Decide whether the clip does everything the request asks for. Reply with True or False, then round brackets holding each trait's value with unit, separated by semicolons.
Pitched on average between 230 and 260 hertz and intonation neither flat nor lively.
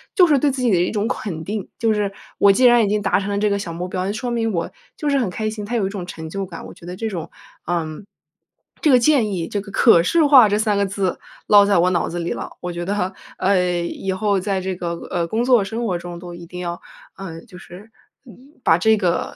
False (195 Hz; 3.7 semitones)